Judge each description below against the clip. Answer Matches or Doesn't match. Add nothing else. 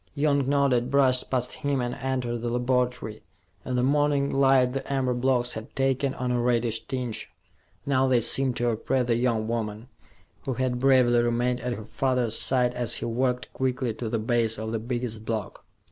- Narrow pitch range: Matches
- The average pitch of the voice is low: Matches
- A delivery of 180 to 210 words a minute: Matches